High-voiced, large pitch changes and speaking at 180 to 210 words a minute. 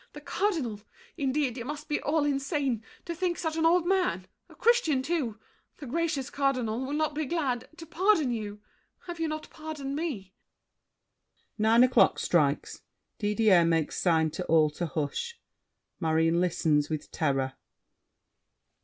No: very high, 265 Hz; wide, 8.9 semitones; average, 140 wpm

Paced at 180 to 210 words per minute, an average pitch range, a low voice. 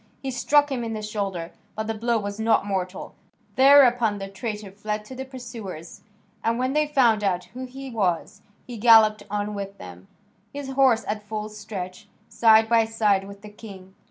No: average, 185 wpm; average, 3.1 semitones; high, 215 Hz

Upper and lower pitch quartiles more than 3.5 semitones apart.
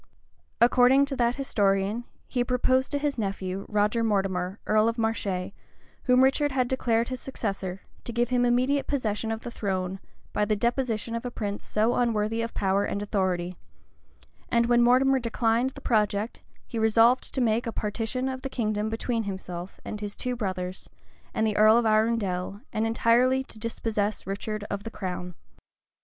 No: average, 3.2 semitones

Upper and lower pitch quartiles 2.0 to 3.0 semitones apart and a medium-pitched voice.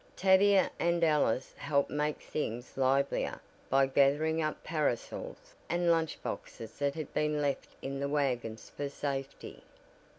Yes: average, 2.7 semitones; medium, 145 Hz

